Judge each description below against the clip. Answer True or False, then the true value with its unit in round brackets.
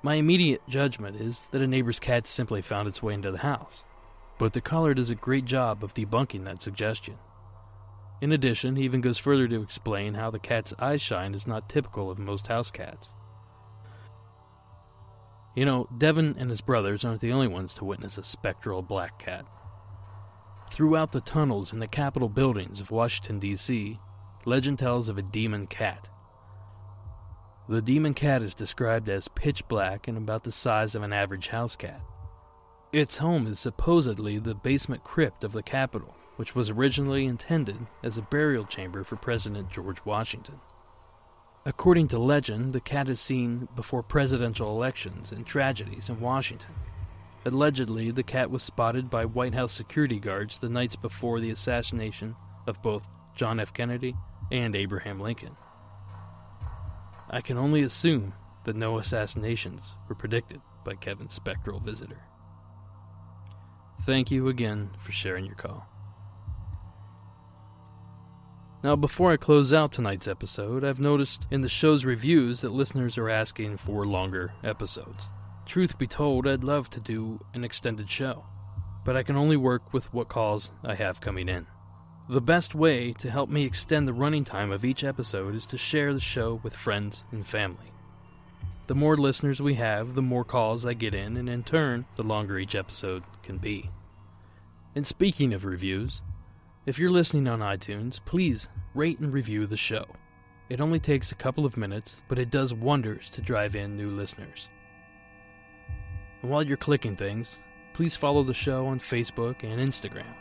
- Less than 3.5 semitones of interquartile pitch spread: False (4.4 semitones)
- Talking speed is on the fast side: False (165 wpm)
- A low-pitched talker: True (110 Hz)